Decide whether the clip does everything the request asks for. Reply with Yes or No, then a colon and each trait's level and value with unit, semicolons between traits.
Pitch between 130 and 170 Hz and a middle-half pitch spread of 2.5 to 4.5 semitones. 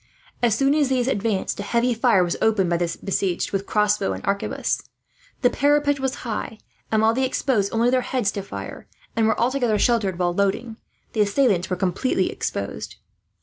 No: high, 220 Hz; average, 4.1 semitones